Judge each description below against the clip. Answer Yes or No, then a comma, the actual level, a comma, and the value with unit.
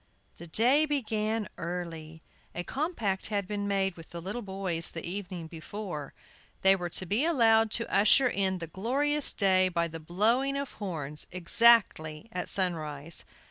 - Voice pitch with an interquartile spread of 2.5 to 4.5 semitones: No, average, 4.9 semitones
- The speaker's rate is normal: Yes, average, 155 wpm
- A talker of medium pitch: No, high, 195 Hz